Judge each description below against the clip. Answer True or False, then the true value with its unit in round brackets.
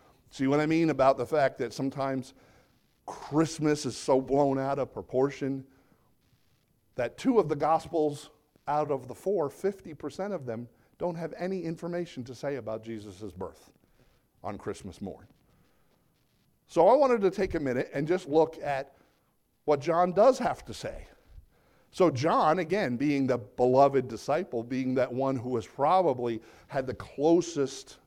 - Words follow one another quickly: False (155 wpm)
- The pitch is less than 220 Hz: True (140 Hz)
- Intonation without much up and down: False (4.1 semitones)